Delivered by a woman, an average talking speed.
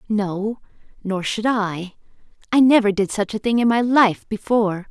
Yes: female; average, 160 wpm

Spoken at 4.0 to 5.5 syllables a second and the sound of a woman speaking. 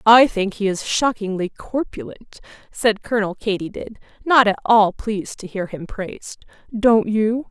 Yes: 4.5 syllables/s; female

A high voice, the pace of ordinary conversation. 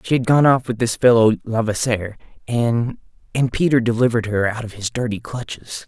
No: low, 115 Hz; average, 185 wpm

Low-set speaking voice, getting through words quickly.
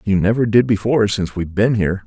Yes: low, 105 Hz; fast, 230 wpm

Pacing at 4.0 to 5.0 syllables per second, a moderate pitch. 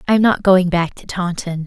No: 5.3 syllables/s; medium, 180 Hz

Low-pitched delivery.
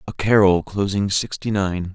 Yes: very low, 95 Hz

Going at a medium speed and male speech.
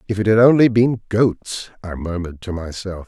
Yes: average, 195 wpm; male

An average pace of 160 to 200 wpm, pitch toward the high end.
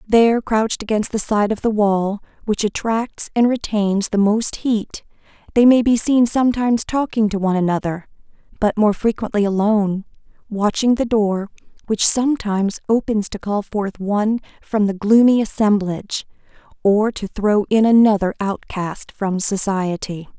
No: average, 145 wpm; high, 210 Hz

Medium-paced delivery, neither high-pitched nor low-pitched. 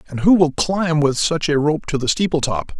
No: fast, 255 wpm; medium, 155 Hz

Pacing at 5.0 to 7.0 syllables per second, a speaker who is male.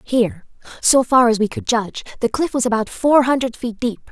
No: 5.6 syllables/s; female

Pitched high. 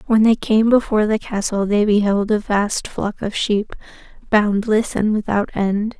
Yes: high, 210 Hz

